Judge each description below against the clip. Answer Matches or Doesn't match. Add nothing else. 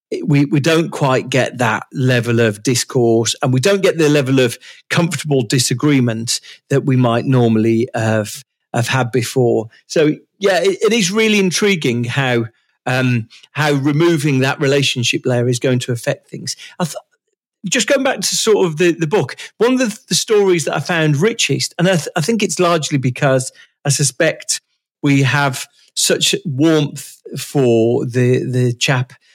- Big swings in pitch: Matches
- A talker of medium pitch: Matches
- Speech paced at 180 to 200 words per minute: Doesn't match